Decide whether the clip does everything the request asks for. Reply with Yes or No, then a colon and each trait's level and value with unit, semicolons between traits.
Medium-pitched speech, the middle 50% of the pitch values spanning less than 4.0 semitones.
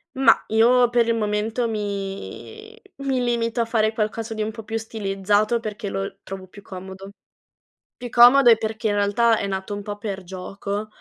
No: high, 215 Hz; narrow, 2.6 semitones